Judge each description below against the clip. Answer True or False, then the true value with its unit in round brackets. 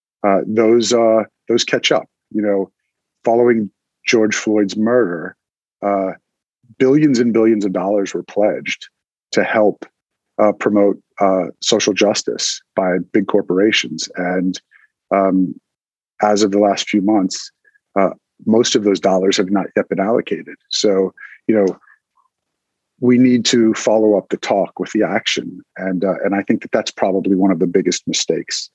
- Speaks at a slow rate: False (155 wpm)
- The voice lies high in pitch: False (105 Hz)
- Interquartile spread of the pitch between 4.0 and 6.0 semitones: False (2.7 semitones)